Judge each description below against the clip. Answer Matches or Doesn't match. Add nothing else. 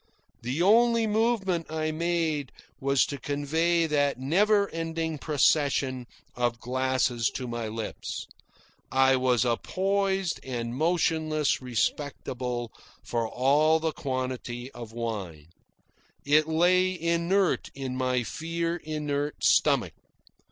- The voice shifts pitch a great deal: Doesn't match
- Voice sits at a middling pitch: Matches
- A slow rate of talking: Matches